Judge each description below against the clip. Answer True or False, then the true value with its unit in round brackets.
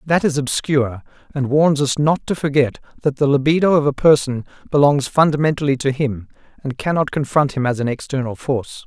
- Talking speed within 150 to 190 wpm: True (185 wpm)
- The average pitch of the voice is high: False (140 Hz)